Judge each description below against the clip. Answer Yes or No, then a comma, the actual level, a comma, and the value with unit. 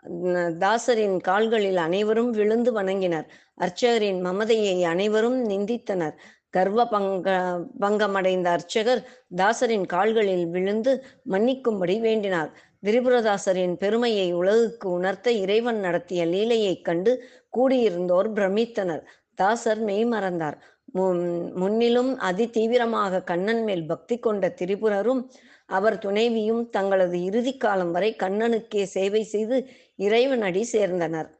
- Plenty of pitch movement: No, average, 4.0 semitones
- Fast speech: No, average, 90 wpm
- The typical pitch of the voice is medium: No, high, 205 Hz